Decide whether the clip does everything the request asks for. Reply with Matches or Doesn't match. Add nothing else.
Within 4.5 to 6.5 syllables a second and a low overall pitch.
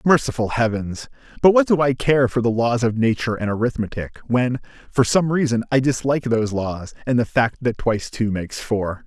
Matches